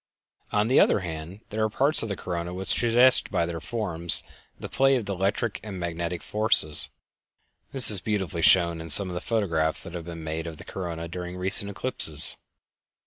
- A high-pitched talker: No, very low, 90 Hz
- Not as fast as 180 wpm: No, average, 190 wpm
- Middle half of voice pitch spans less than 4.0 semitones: No, average, 4.3 semitones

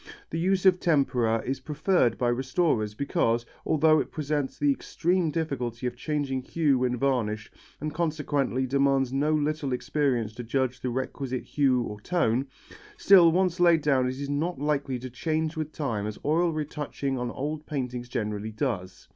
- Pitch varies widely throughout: No, average, 3.8 semitones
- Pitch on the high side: No, medium, 140 Hz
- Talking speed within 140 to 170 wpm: Yes, average, 165 wpm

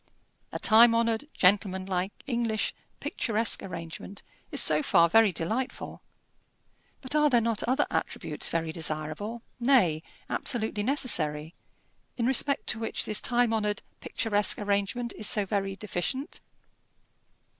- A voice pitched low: No, high, 215 Hz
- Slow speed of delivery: Yes, slow, 125 wpm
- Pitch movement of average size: Yes, average, 4.0 semitones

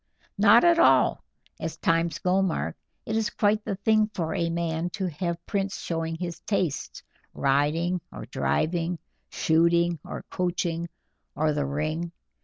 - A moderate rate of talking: Yes, average, 145 wpm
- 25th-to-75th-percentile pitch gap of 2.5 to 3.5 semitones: Yes, average, 2.8 semitones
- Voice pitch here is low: No, medium, 170 Hz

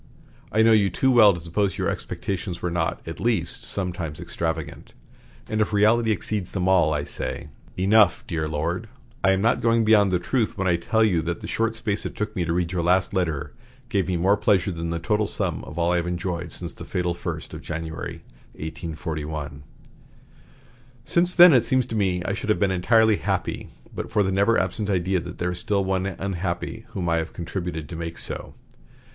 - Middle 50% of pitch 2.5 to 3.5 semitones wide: No, average, 3.9 semitones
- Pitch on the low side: Yes, very low, 95 Hz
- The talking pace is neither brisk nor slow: No, fast, 210 wpm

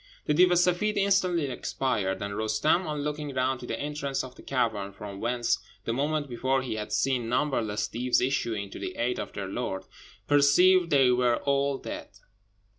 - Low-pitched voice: Yes, low, 130 Hz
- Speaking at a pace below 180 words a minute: No, average, 185 wpm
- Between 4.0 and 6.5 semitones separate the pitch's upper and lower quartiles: Yes, average, 4.5 semitones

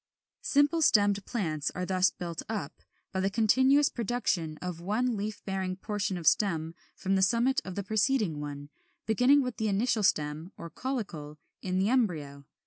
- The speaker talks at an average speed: Yes, average, 165 wpm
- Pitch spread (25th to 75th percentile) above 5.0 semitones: Yes, wide, 5.5 semitones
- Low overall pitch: No, high, 195 Hz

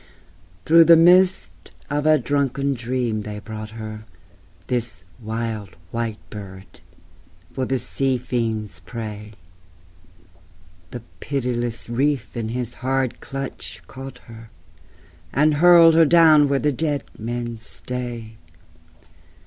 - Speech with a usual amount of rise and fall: Yes, average, 4.1 semitones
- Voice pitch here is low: Yes, low, 120 Hz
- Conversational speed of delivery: No, slow, 115 wpm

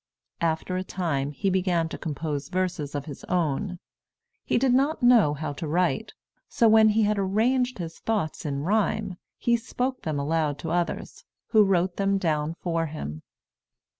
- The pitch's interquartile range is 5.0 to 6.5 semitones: Yes, wide, 5.4 semitones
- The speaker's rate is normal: Yes, average, 165 wpm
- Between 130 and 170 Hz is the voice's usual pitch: No, medium, 180 Hz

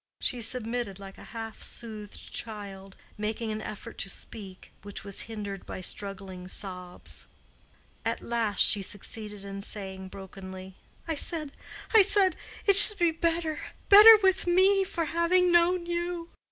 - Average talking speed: No, slow, 130 wpm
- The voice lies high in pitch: Yes, high, 225 Hz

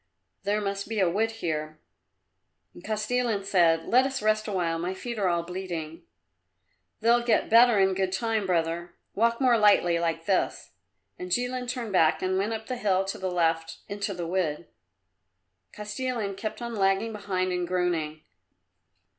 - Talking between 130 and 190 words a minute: Yes, average, 165 wpm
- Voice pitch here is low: No, high, 195 Hz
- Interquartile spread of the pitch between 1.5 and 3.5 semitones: No, average, 4.1 semitones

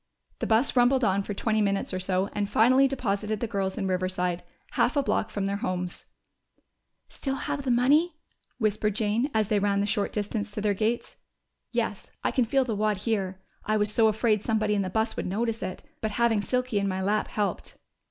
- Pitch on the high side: Yes, high, 215 Hz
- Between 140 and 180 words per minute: No, fast, 205 wpm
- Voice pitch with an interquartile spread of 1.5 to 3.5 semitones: Yes, average, 2.8 semitones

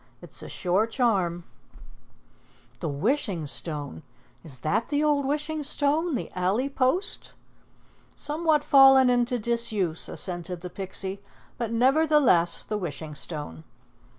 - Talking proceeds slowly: Yes, slow, 125 wpm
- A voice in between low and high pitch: No, high, 225 Hz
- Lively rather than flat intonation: Yes, wide, 8.1 semitones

